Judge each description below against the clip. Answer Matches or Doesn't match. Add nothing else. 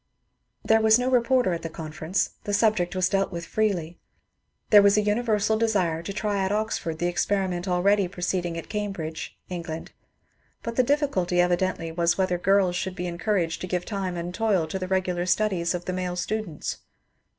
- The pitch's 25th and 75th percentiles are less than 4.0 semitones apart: Matches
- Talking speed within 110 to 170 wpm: Doesn't match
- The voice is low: Doesn't match